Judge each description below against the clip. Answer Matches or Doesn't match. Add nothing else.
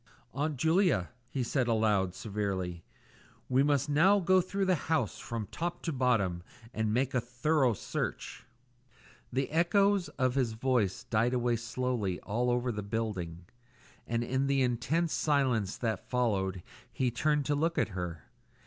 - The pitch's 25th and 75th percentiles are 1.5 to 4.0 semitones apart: Doesn't match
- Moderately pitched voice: Doesn't match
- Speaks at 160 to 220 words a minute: Doesn't match